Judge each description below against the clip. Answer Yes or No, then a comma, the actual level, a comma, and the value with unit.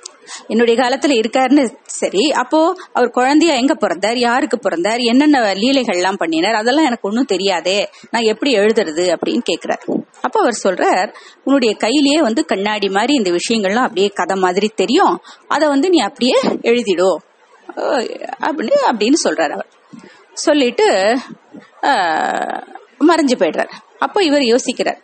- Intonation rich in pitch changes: Yes, wide, 6.6 semitones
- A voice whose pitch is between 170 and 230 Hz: No, very high, 250 Hz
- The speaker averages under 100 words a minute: No, average, 125 wpm